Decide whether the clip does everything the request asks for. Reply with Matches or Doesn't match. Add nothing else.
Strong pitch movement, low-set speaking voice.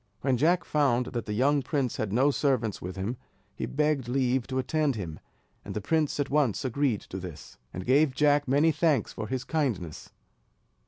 Doesn't match